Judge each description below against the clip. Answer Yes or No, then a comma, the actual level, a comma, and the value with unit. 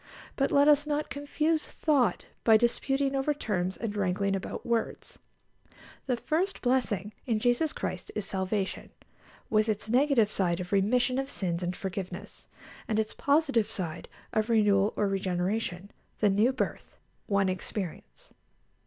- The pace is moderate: Yes, average, 145 wpm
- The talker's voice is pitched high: Yes, high, 215 Hz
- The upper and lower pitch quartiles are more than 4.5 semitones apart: Yes, wide, 5.6 semitones